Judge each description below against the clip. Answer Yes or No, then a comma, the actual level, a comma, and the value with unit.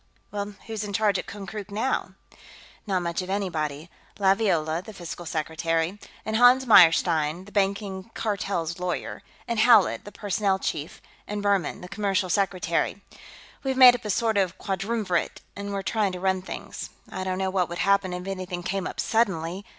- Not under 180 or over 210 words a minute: No, average, 170 wpm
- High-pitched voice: Yes, high, 195 Hz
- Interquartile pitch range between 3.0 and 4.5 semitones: No, narrow, 2.6 semitones